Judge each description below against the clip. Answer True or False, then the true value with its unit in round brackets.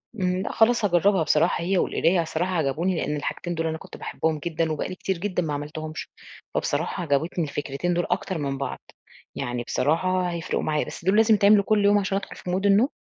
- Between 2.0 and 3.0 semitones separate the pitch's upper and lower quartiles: False (3.7 semitones)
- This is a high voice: False (175 Hz)